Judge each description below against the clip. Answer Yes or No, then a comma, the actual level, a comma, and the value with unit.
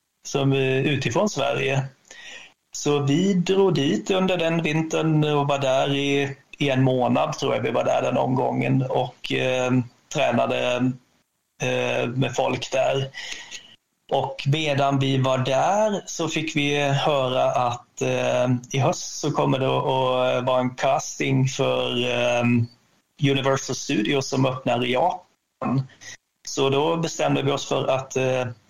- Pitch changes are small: Yes, narrow, 2.3 semitones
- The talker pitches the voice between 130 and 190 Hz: Yes, low, 135 Hz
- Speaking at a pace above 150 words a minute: No, average, 140 wpm